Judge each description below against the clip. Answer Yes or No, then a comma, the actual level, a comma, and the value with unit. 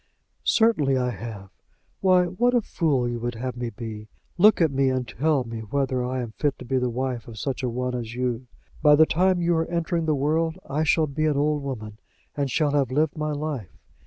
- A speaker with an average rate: No, fast, 220 wpm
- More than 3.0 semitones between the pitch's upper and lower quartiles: Yes, average, 4.3 semitones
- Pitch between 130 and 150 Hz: Yes, low, 135 Hz